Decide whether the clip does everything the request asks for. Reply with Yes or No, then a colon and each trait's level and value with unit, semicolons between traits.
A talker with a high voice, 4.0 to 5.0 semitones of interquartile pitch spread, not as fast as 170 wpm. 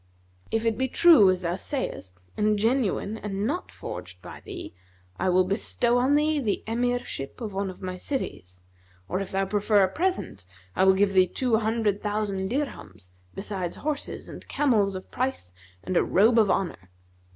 No: high, 205 Hz; average, 4.6 semitones; average, 175 wpm